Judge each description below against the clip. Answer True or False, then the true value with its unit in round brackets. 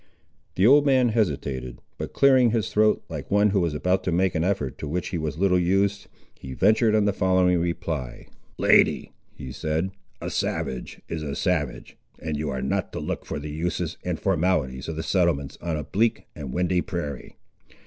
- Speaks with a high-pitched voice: False (85 Hz)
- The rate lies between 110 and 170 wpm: False (190 wpm)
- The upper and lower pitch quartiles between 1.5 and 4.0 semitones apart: False (4.7 semitones)